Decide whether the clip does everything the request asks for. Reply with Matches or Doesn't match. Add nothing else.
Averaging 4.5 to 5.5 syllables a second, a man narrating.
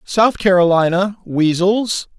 Doesn't match